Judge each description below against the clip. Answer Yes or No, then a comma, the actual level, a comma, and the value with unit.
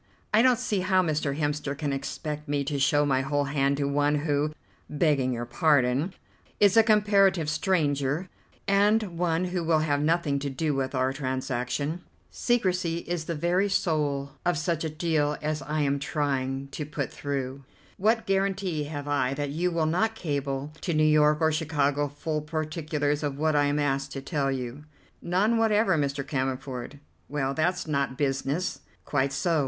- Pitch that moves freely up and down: No, average, 3.4 semitones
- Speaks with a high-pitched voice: No, medium, 150 Hz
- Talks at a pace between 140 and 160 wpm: No, average, 170 wpm